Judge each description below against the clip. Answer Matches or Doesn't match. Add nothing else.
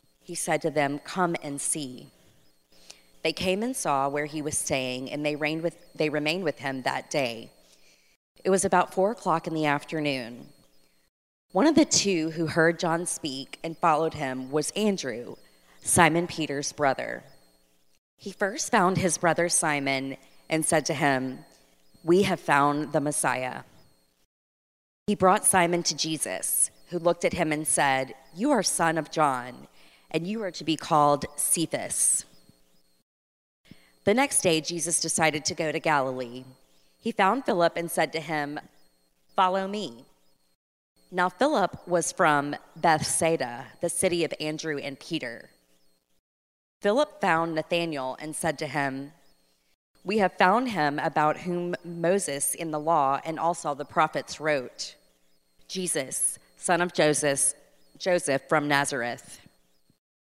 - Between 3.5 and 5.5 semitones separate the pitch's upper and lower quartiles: Matches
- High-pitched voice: Doesn't match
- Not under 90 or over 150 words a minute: Matches